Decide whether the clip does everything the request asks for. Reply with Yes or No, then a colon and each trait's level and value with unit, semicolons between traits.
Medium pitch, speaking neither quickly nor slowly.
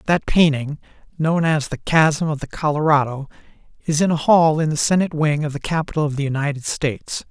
Yes: medium, 150 Hz; average, 195 wpm